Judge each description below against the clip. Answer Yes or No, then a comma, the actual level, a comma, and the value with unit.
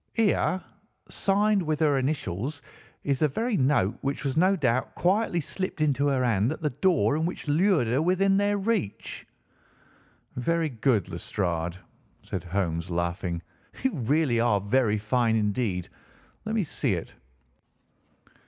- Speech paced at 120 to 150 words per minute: Yes, average, 145 wpm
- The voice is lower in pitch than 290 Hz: Yes, medium, 140 Hz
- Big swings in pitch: Yes, wide, 8.4 semitones